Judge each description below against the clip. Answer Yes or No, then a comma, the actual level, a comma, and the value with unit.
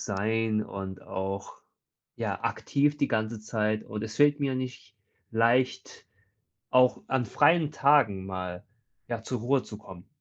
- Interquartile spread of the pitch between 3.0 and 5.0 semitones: Yes, average, 4.1 semitones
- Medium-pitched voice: No, low, 115 Hz